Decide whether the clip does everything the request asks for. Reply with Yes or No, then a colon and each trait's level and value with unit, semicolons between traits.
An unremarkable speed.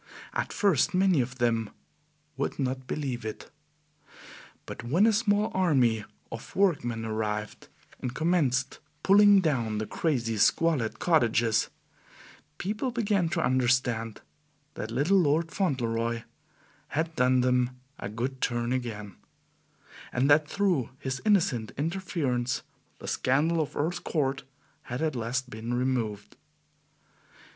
No: slow, 120 wpm